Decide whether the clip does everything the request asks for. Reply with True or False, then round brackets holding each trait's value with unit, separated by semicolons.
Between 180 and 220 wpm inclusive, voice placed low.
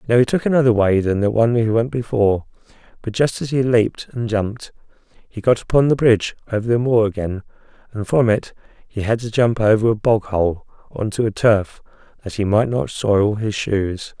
True (205 wpm; 110 Hz)